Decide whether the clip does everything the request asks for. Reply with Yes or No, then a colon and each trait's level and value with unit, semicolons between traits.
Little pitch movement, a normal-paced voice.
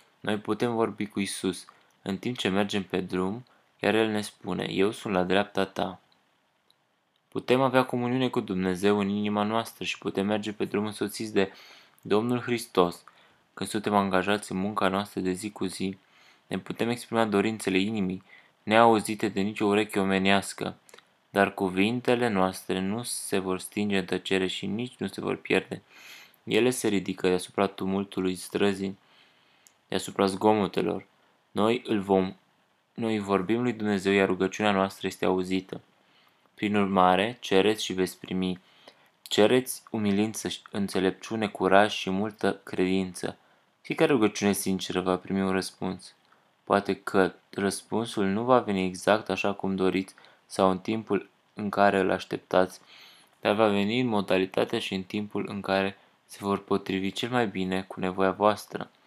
Yes: narrow, 2.1 semitones; average, 150 wpm